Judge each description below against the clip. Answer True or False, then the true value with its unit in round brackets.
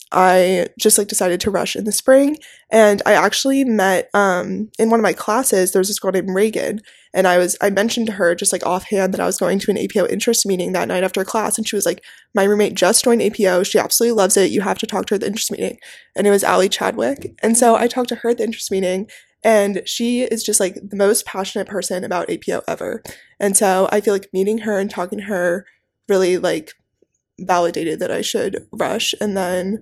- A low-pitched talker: False (200 Hz)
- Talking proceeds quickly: True (235 wpm)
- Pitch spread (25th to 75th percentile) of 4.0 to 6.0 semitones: False (2.8 semitones)